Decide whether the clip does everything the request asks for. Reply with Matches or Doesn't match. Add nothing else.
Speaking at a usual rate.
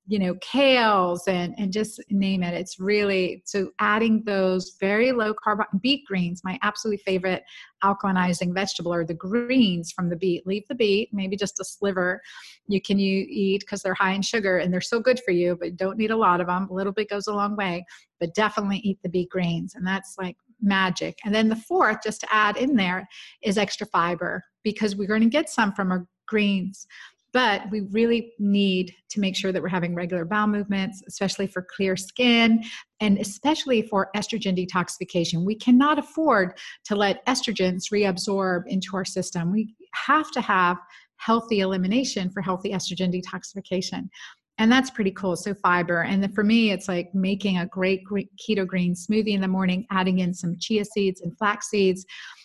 Matches